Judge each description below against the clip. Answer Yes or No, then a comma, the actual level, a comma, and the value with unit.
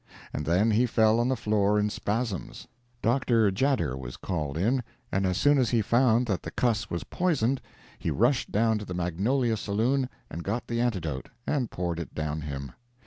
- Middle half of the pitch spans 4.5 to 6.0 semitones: Yes, wide, 5.5 semitones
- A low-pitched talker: Yes, low, 110 Hz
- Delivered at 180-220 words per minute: Yes, average, 190 wpm